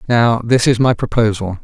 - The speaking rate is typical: Yes, average, 185 wpm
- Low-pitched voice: Yes, low, 115 Hz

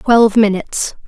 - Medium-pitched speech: No, high, 215 Hz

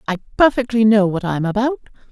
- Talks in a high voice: Yes, high, 215 Hz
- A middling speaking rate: Yes, average, 170 wpm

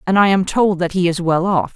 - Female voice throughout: Yes, female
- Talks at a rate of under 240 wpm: No, fast, 305 wpm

